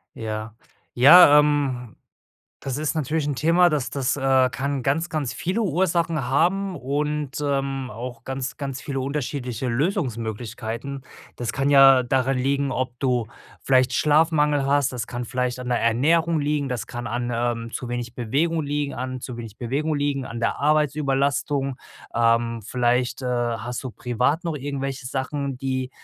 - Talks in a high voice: No, low, 135 Hz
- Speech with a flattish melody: No, average, 3.0 semitones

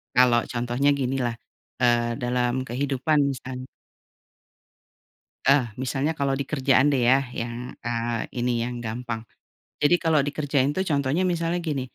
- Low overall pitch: Yes, low, 130 Hz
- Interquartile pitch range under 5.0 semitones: Yes, average, 2.9 semitones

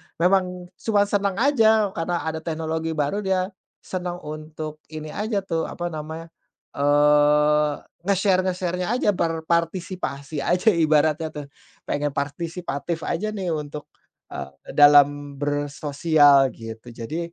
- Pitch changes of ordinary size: Yes, average, 3.7 semitones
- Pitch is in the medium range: Yes, medium, 160 Hz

